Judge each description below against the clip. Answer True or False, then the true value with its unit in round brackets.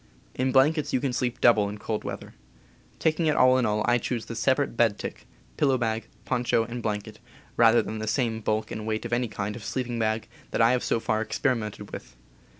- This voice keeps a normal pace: False (220 wpm)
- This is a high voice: False (115 Hz)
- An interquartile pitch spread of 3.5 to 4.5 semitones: False (2.6 semitones)